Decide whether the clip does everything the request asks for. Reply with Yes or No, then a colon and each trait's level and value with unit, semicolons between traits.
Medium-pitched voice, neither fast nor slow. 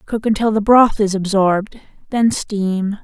No: high, 205 Hz; average, 160 wpm